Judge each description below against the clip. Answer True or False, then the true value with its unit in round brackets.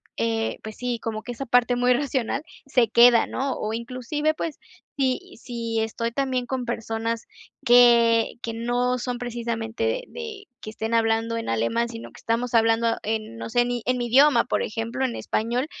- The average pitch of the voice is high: True (235 Hz)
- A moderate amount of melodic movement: False (1.7 semitones)